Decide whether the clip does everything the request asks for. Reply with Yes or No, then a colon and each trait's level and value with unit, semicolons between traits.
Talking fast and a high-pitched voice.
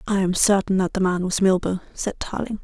Yes: fast, 230 wpm; high, 195 Hz